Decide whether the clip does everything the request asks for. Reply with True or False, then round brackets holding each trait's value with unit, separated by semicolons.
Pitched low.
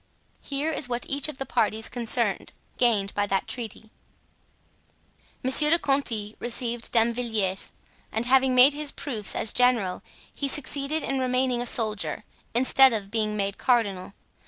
False (240 Hz)